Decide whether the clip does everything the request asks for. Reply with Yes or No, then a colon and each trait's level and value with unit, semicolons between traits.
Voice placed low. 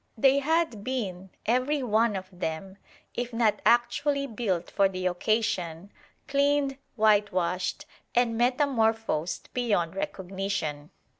No: high, 220 Hz